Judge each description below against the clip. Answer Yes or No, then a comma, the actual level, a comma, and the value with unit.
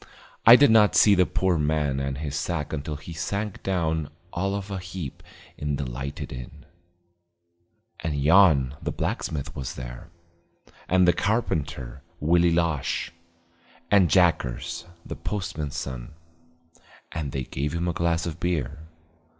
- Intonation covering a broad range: No, average, 4.2 semitones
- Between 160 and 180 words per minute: No, average, 145 wpm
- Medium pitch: No, very low, 80 Hz